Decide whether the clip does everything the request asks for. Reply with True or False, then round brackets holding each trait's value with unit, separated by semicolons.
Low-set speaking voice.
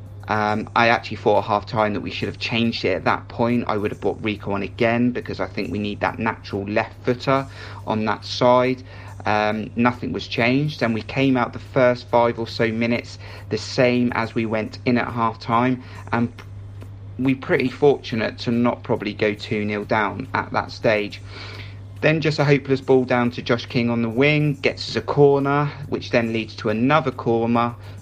True (115 Hz)